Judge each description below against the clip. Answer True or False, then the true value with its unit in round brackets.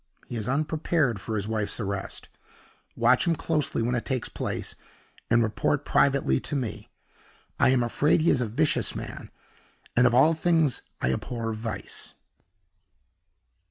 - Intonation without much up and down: False (4.9 semitones)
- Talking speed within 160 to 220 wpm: False (150 wpm)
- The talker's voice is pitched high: False (125 Hz)